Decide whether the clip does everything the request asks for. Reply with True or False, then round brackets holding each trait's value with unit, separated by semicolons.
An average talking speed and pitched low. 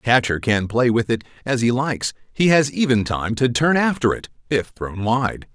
False (215 wpm; 120 Hz)